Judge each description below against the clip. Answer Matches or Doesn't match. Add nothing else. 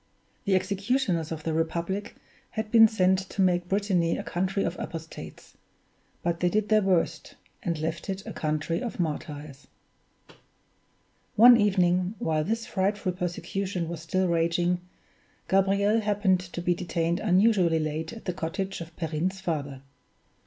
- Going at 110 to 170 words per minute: Matches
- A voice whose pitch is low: Doesn't match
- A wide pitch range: Doesn't match